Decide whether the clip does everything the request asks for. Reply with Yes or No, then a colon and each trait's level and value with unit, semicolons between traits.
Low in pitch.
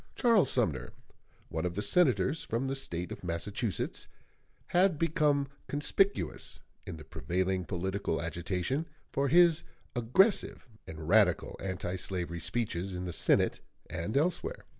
Yes: low, 100 Hz